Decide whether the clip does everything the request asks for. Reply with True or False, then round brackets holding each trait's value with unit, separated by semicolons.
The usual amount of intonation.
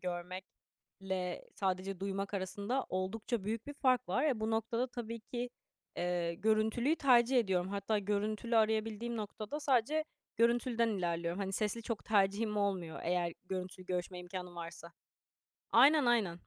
True (4.1 semitones)